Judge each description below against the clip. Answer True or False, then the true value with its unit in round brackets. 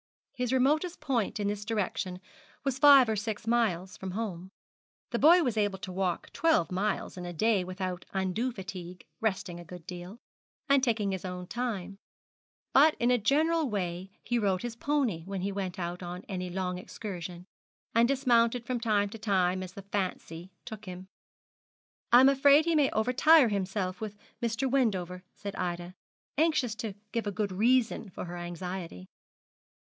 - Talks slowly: False (165 wpm)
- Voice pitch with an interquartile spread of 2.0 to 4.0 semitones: False (4.8 semitones)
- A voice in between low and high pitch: False (205 Hz)